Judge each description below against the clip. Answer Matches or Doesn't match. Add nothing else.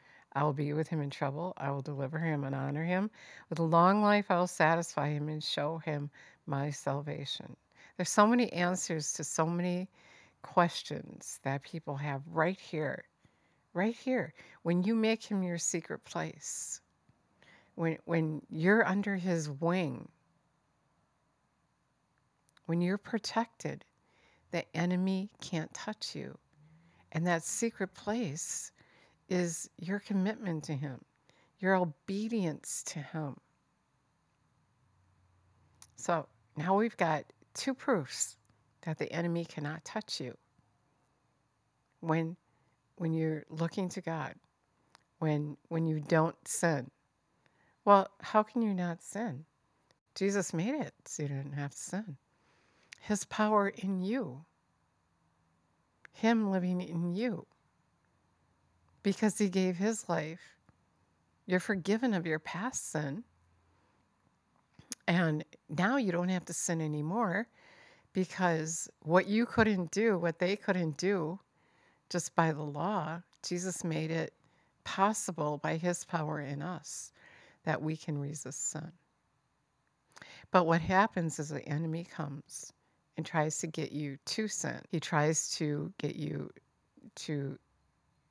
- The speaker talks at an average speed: Doesn't match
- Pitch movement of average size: Matches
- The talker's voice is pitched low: Doesn't match